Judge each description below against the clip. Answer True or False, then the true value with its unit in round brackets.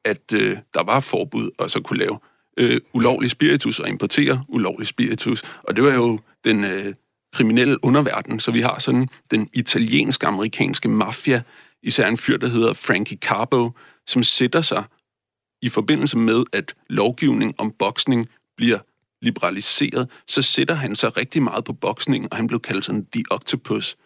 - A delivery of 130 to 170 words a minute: True (160 wpm)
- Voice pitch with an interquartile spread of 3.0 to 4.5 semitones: False (2.4 semitones)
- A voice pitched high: False (120 Hz)